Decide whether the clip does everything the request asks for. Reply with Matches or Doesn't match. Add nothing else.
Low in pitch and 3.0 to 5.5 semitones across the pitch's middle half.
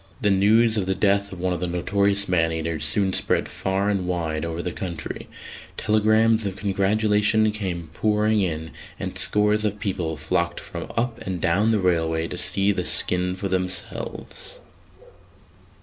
Matches